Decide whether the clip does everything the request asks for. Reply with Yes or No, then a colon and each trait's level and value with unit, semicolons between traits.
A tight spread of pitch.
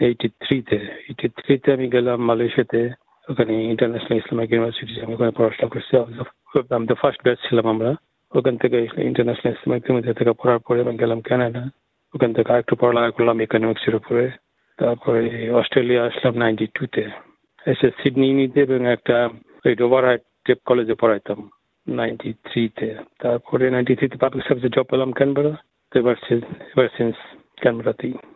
Yes: narrow, 1.6 semitones